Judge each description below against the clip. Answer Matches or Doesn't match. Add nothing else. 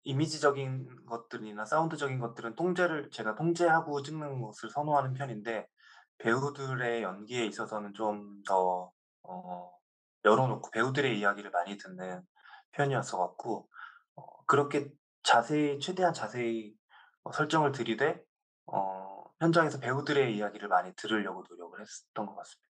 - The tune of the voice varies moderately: Doesn't match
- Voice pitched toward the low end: Matches